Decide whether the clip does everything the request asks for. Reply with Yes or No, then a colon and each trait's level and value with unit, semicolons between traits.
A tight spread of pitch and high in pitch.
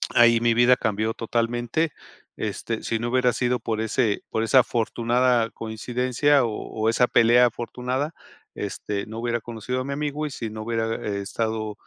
No: narrow, 1.9 semitones; low, 115 Hz